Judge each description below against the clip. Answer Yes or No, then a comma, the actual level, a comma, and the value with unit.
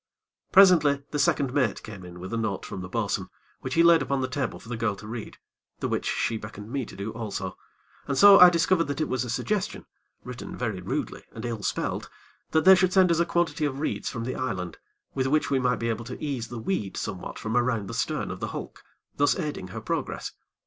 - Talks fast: Yes, fast, 230 wpm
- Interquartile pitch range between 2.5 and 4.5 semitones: No, wide, 5.6 semitones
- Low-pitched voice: Yes, low, 125 Hz